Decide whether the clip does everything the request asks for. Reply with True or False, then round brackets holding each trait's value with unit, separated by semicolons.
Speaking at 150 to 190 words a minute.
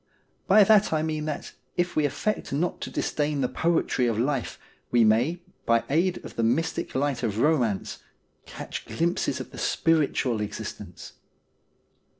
True (155 wpm)